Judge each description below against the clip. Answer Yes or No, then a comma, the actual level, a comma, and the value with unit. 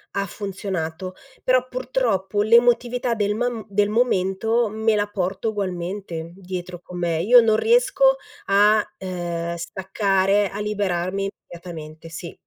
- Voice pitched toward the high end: Yes, high, 200 Hz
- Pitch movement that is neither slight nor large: Yes, average, 3.7 semitones